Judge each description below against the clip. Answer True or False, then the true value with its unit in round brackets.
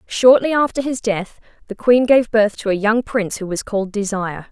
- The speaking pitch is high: True (215 Hz)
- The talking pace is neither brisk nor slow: False (215 wpm)